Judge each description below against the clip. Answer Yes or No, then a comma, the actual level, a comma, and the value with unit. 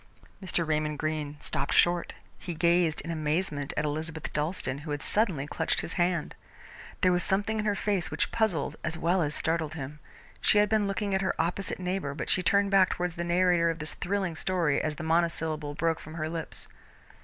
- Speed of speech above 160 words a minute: Yes, average, 200 wpm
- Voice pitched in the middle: Yes, medium, 165 Hz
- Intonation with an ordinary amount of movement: Yes, average, 3.2 semitones